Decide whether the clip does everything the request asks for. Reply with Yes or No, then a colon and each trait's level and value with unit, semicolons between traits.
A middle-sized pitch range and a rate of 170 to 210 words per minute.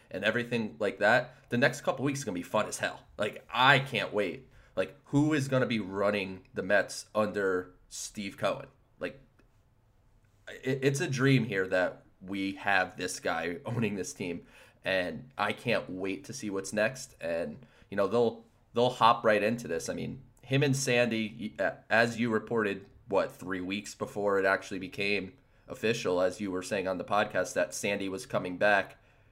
Yes: average, 3.9 semitones; average, 180 wpm